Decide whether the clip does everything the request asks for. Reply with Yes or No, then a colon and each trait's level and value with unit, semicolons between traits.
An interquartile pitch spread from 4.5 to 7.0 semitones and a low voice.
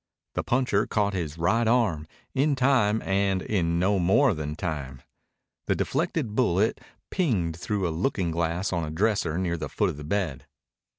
Yes: average, 5.0 semitones; very low, 95 Hz